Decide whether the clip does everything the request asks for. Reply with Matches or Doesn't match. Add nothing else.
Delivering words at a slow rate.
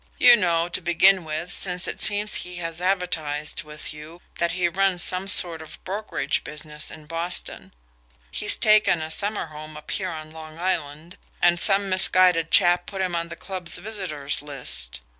Doesn't match